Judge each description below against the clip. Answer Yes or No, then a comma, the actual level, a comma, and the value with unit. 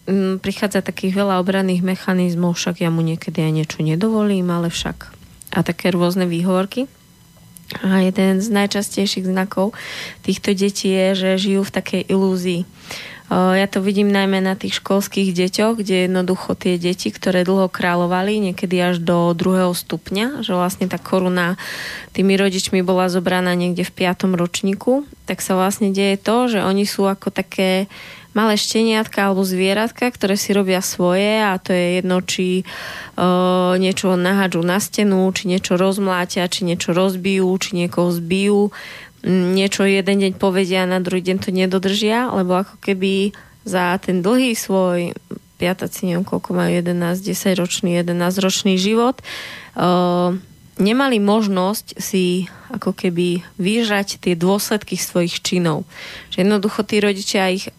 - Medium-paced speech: Yes, average, 150 wpm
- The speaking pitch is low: No, high, 190 Hz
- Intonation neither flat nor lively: No, narrow, 1.7 semitones